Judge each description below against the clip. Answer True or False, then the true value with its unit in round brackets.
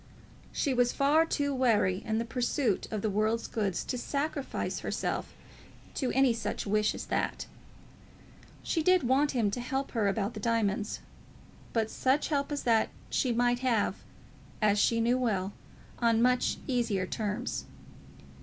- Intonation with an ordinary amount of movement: True (3.6 semitones)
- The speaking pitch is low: False (235 Hz)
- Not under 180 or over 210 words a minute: False (155 wpm)